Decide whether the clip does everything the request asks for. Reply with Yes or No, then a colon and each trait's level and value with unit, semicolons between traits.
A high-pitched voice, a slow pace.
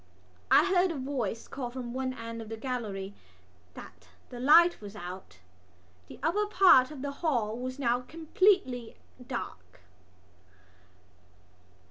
Yes: very high, 250 Hz; slow, 130 wpm